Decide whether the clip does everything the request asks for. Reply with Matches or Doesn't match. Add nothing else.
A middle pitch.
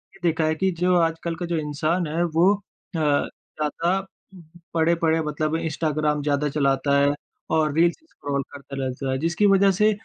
Matches